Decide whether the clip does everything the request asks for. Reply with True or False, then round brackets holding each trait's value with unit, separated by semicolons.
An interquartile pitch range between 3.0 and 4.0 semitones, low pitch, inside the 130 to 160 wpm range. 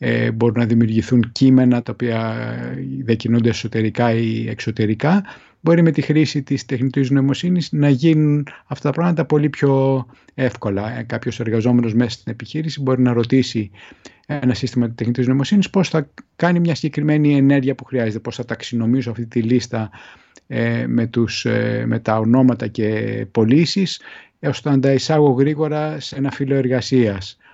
True (3.7 semitones; 125 Hz; 150 wpm)